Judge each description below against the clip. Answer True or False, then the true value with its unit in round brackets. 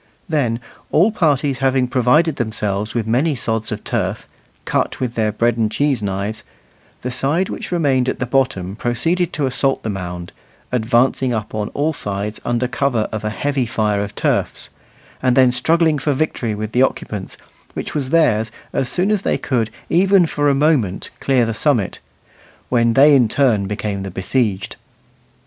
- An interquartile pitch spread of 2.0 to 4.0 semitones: False (4.8 semitones)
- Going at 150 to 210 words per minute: True (170 wpm)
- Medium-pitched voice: False (125 Hz)